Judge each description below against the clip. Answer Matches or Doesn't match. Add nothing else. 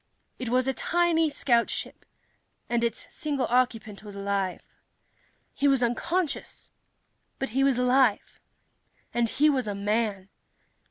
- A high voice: Matches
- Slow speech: Matches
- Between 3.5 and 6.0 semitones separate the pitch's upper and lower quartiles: Matches